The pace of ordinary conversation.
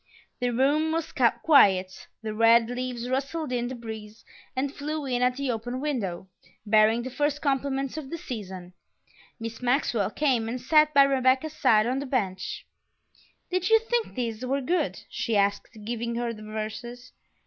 Yes: average, 165 wpm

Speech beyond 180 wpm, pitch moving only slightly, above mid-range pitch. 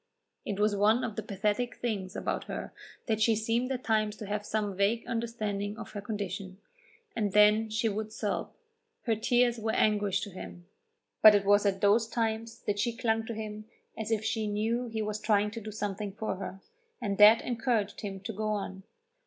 Yes: average, 195 wpm; narrow, 1.6 semitones; high, 215 Hz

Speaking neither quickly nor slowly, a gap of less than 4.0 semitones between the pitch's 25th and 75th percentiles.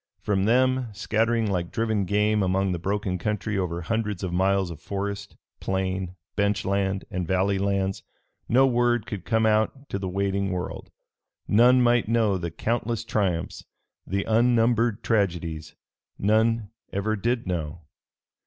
Yes: average, 145 wpm; average, 3.1 semitones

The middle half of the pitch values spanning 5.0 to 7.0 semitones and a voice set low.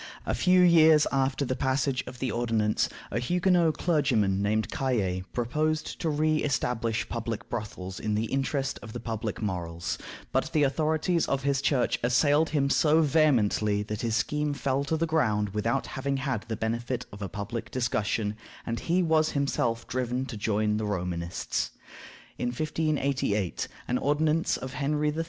Yes: wide, 5.5 semitones; low, 130 Hz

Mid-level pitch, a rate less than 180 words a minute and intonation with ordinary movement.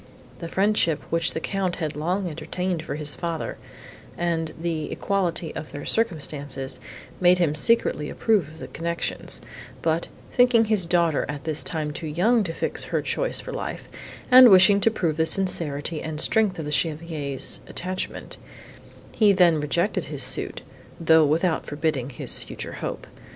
Yes: medium, 165 Hz; average, 160 wpm; average, 3.4 semitones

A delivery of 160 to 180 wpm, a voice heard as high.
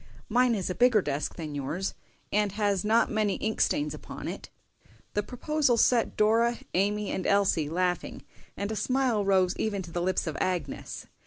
Yes: average, 175 wpm; high, 200 Hz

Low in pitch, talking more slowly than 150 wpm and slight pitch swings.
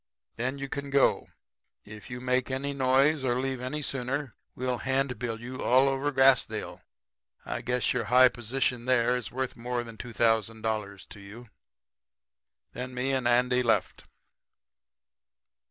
Yes: low, 125 Hz; average, 140 wpm; narrow, 2.0 semitones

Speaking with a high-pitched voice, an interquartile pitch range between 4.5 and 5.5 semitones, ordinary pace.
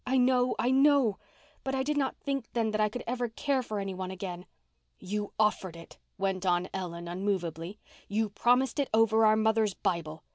Yes: high, 215 Hz; average, 4.9 semitones; average, 180 wpm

